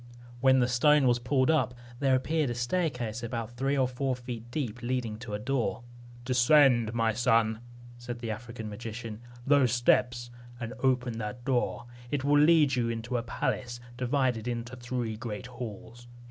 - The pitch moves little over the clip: Yes, narrow, 1.9 semitones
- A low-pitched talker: Yes, low, 120 Hz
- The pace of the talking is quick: No, average, 165 wpm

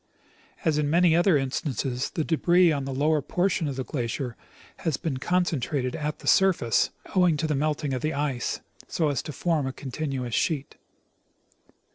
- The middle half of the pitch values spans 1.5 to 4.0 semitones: Yes, average, 3.5 semitones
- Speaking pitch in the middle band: Yes, medium, 150 Hz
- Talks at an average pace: Yes, average, 170 wpm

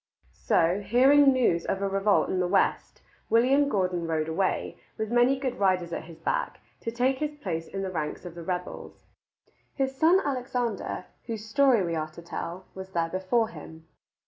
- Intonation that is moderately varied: No, wide, 6.6 semitones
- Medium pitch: No, high, 195 Hz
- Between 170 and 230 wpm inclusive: Yes, average, 180 wpm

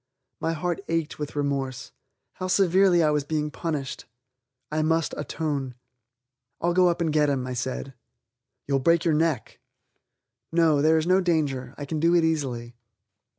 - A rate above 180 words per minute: No, average, 160 wpm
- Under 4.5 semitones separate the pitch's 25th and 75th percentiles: Yes, average, 3.1 semitones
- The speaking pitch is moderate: Yes, medium, 155 Hz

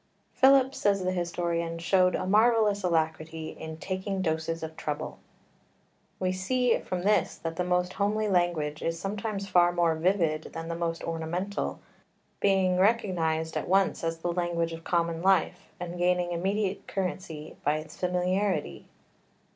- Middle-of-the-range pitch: Yes, medium, 180 Hz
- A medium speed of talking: Yes, average, 145 wpm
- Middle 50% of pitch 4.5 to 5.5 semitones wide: No, average, 2.8 semitones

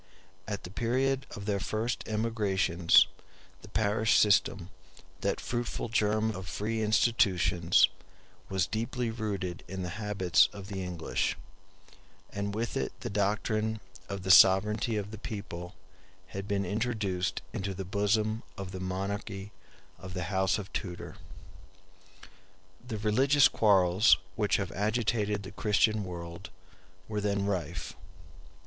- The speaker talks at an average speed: No, slow, 130 wpm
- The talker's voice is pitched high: No, low, 100 Hz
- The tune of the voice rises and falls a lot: No, narrow, 2.4 semitones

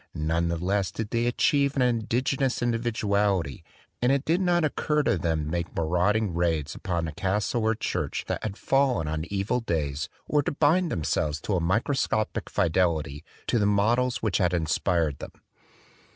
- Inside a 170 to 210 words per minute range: Yes, average, 175 wpm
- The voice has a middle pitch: No, low, 100 Hz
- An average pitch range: No, wide, 6.7 semitones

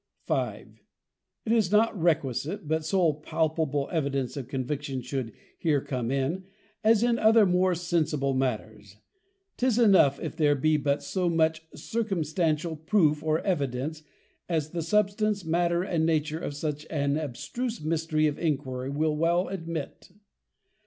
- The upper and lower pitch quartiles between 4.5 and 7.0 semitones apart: No, average, 3.8 semitones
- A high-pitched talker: No, medium, 160 Hz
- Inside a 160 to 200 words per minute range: No, average, 140 wpm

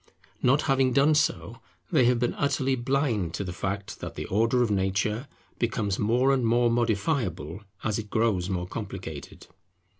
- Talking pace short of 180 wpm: Yes, average, 160 wpm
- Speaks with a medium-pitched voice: No, low, 115 Hz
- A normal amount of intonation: Yes, average, 4.4 semitones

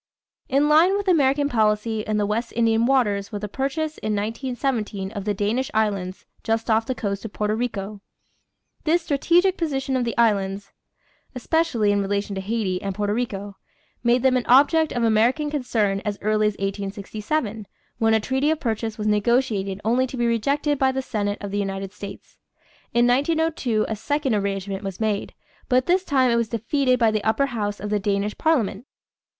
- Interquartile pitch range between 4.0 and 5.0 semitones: Yes, average, 4.5 semitones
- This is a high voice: Yes, high, 225 Hz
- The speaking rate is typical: Yes, average, 185 wpm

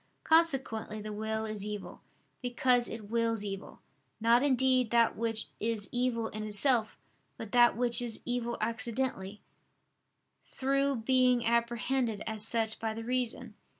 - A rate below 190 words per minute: Yes, slow, 135 wpm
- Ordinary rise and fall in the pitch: No, narrow, 2.2 semitones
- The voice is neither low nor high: No, high, 230 Hz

